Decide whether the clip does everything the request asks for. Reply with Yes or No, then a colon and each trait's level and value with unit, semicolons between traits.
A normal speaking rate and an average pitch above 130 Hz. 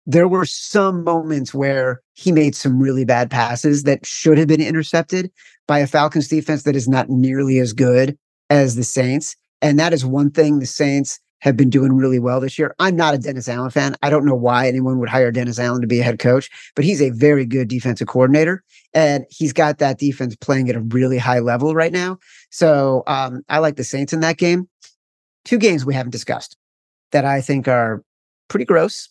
No: fast, 210 wpm; medium, 140 Hz